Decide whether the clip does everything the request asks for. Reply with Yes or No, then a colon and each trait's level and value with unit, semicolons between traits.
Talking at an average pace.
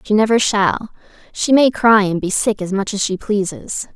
Yes: average, 195 wpm